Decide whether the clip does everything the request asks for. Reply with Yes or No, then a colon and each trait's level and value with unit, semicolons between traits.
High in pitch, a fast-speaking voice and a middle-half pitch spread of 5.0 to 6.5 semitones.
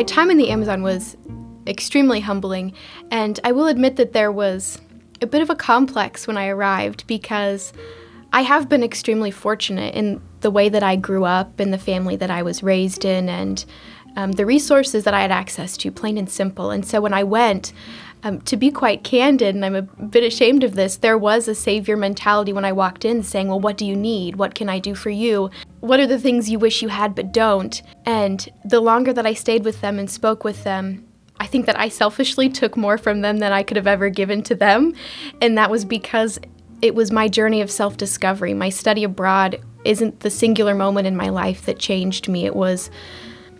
No: high, 210 Hz; fast, 220 wpm; average, 2.9 semitones